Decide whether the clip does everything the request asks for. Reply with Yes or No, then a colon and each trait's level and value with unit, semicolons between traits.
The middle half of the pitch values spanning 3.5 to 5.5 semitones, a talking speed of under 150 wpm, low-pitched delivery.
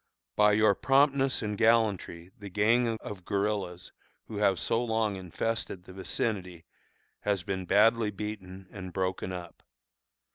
No: average, 3.1 semitones; slow, 135 wpm; low, 100 Hz